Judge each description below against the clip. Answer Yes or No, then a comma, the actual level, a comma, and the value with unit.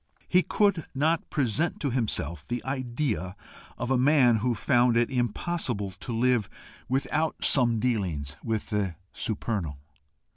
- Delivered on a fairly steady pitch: No, average, 4.4 semitones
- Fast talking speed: No, slow, 135 wpm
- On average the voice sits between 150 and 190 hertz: No, low, 120 Hz